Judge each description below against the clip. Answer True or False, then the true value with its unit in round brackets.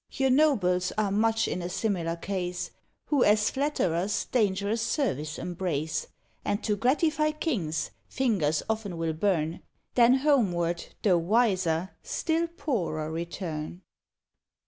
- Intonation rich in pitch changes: True (6.1 semitones)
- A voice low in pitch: False (195 Hz)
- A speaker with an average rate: False (120 wpm)